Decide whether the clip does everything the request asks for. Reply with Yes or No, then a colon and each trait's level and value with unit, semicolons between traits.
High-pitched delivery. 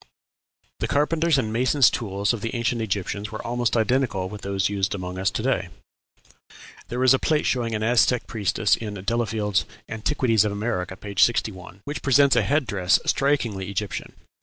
No: low, 110 Hz